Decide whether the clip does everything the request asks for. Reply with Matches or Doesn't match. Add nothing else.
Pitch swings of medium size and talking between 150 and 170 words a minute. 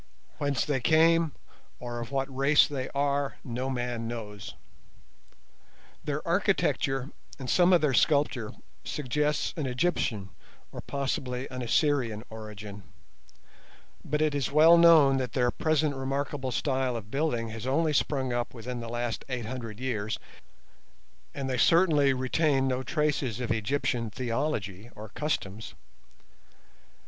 Doesn't match